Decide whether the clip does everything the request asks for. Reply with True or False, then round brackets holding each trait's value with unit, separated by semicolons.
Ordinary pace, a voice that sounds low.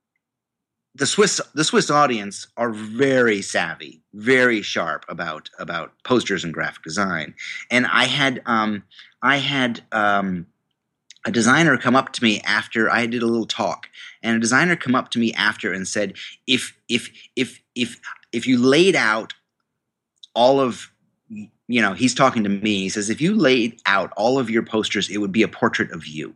True (180 wpm; 115 Hz)